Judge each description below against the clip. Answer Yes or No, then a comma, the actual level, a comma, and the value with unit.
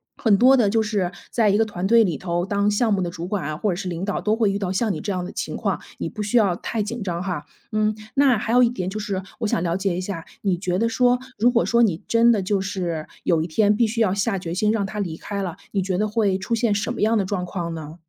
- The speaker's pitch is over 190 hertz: Yes, high, 200 Hz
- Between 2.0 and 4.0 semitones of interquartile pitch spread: Yes, average, 3.4 semitones